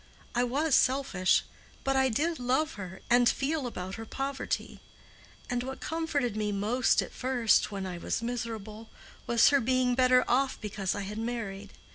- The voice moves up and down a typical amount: Yes, average, 3.9 semitones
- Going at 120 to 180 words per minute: Yes, average, 165 wpm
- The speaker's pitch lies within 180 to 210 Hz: No, high, 245 Hz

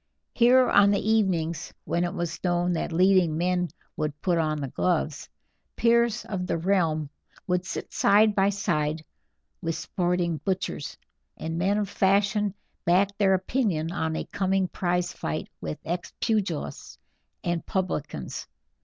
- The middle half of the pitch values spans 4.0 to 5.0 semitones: No, average, 3.4 semitones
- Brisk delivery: No, average, 145 wpm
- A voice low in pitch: No, medium, 180 Hz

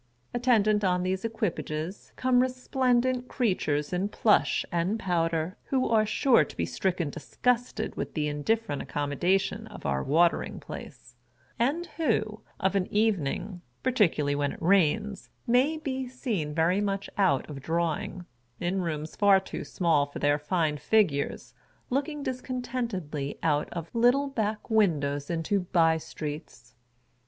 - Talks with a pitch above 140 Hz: Yes, high, 190 Hz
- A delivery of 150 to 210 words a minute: No, average, 140 wpm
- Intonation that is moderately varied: No, wide, 6.8 semitones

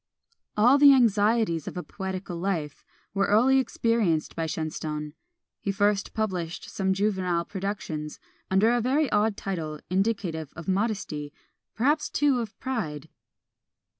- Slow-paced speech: Yes, slow, 130 wpm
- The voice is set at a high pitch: Yes, high, 195 Hz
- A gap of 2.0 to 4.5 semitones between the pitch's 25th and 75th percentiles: No, average, 5.1 semitones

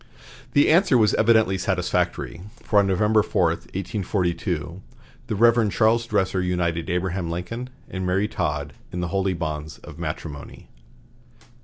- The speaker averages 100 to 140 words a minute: Yes, slow, 135 wpm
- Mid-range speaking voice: No, very low, 95 Hz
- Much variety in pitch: No, average, 3.9 semitones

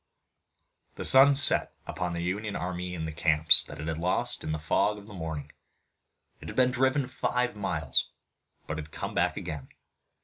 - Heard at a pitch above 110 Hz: No, very low, 90 Hz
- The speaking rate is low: No, average, 180 wpm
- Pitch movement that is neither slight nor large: No, wide, 5.7 semitones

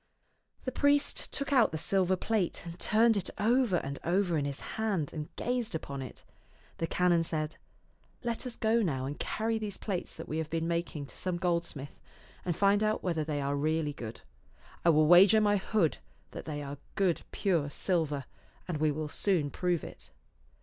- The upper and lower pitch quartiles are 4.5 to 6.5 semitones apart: Yes, average, 5.2 semitones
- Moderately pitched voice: Yes, medium, 175 Hz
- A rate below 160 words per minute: No, average, 190 wpm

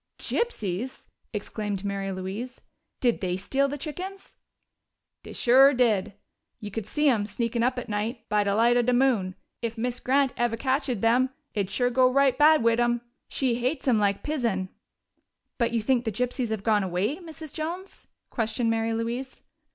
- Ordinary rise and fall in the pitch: Yes, average, 3.9 semitones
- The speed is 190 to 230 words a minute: No, average, 175 wpm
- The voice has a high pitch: Yes, high, 235 Hz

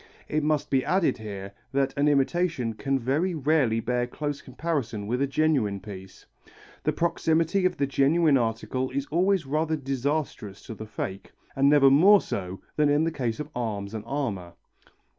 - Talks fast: No, average, 170 wpm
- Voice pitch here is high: No, low, 135 Hz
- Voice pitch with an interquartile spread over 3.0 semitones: Yes, average, 5.3 semitones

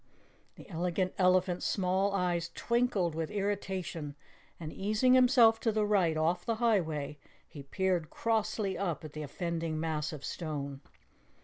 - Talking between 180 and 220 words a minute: No, average, 140 wpm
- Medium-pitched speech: Yes, medium, 180 Hz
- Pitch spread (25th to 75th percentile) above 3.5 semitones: Yes, average, 4.4 semitones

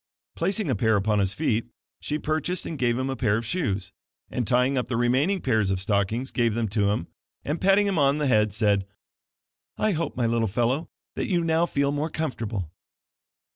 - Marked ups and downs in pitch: Yes, wide, 6.3 semitones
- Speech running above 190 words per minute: Yes, fast, 205 wpm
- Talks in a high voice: No, low, 125 Hz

